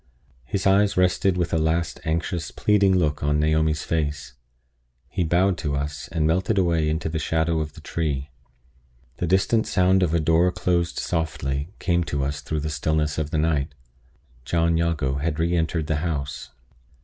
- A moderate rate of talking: Yes, average, 175 wpm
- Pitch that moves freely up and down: No, narrow, 2.5 semitones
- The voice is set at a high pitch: No, very low, 80 Hz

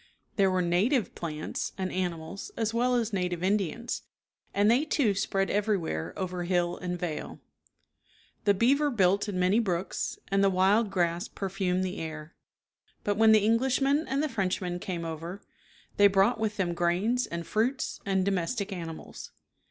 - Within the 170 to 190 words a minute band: No, average, 160 wpm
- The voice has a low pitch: No, high, 195 Hz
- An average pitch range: Yes, average, 3.7 semitones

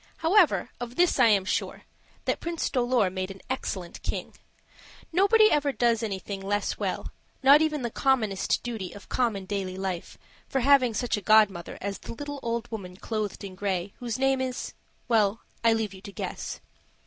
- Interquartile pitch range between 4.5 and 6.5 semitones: Yes, average, 5.1 semitones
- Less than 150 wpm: No, average, 175 wpm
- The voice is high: Yes, high, 225 Hz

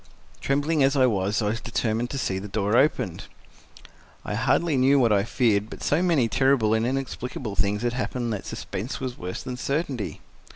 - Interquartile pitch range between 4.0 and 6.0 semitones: Yes, average, 4.3 semitones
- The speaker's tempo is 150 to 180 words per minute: No, average, 190 wpm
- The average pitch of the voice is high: No, low, 120 Hz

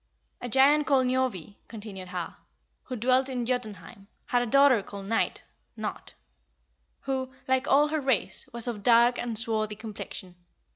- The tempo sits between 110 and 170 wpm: Yes, average, 160 wpm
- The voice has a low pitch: No, high, 240 Hz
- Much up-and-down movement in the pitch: No, average, 3.7 semitones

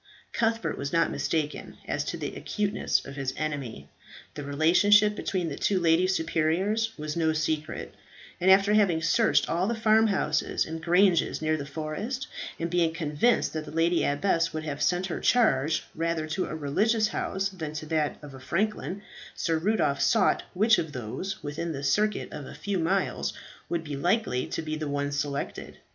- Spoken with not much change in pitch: No, average, 4.6 semitones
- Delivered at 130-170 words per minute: No, average, 180 wpm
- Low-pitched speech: No, medium, 165 Hz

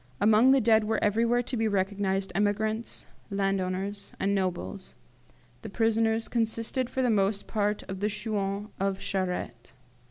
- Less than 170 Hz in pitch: No, high, 205 Hz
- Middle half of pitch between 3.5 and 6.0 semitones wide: No, narrow, 2.4 semitones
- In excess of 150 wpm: No, average, 145 wpm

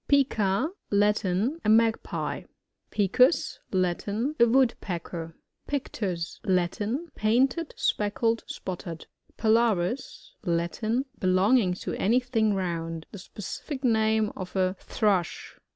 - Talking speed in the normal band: No, slow, 115 wpm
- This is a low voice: No, high, 210 Hz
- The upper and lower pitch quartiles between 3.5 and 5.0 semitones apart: Yes, average, 4.4 semitones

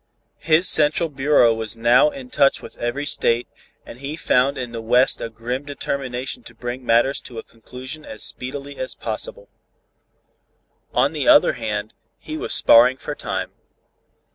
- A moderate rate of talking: Yes, average, 160 wpm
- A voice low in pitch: Yes, low, 130 Hz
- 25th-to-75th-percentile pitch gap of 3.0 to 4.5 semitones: Yes, average, 3.7 semitones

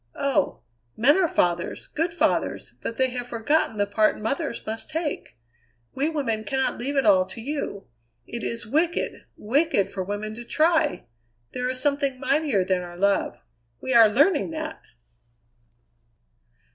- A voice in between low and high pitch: No, very high, 250 Hz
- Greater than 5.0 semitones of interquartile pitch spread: Yes, wide, 5.6 semitones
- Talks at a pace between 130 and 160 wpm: Yes, average, 150 wpm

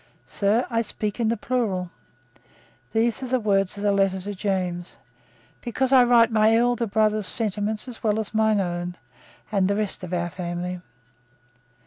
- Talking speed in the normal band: Yes, average, 165 wpm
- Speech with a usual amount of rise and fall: Yes, average, 3.4 semitones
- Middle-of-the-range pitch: No, high, 210 Hz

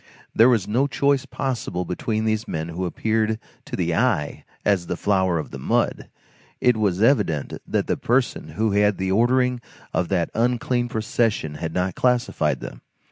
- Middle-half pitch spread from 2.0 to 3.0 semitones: No, average, 5.2 semitones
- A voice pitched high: No, low, 110 Hz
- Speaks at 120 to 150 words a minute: No, average, 175 wpm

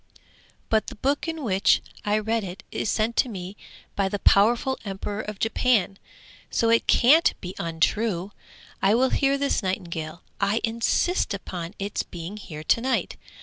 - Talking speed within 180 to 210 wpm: No, average, 160 wpm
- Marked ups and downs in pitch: No, average, 3.5 semitones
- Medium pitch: No, high, 210 Hz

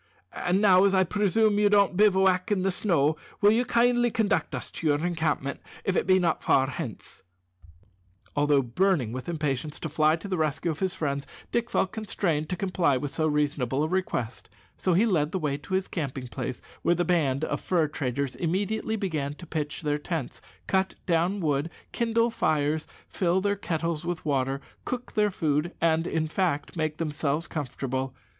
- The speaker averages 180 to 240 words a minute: Yes, average, 185 wpm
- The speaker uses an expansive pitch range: No, average, 4.6 semitones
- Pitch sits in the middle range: Yes, medium, 165 Hz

